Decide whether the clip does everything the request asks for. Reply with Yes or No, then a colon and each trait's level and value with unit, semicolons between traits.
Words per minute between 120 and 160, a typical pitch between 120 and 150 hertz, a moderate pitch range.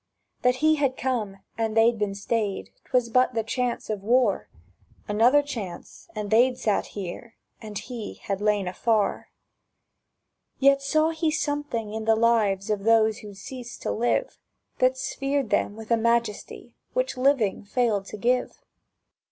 No: average, 150 wpm; high, 230 Hz; average, 3.5 semitones